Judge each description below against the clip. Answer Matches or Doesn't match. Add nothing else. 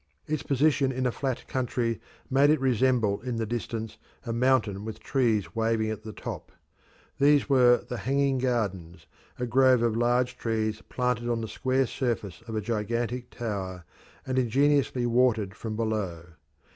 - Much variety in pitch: Doesn't match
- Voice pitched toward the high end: Doesn't match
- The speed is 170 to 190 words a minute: Doesn't match